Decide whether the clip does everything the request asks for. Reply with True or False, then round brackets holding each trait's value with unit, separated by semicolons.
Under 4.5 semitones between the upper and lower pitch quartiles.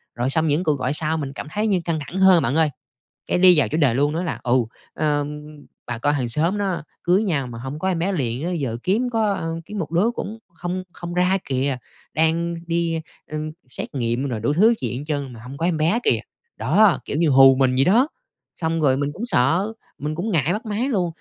False (4.9 semitones)